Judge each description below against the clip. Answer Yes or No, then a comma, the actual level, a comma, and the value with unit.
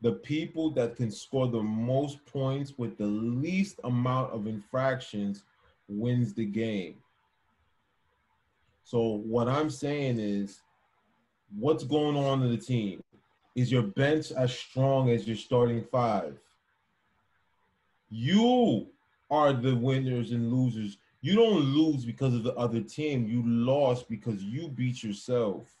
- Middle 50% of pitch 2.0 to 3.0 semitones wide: No, average, 3.8 semitones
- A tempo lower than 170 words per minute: Yes, slow, 135 wpm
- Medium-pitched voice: No, low, 120 Hz